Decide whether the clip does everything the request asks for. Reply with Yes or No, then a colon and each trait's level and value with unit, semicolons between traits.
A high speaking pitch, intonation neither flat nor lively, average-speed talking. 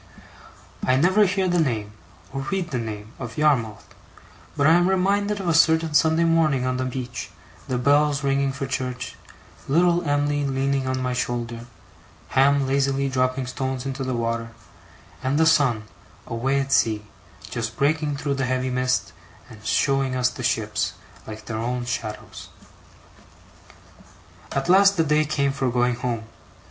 No: low, 135 Hz; average, 3.5 semitones; average, 155 wpm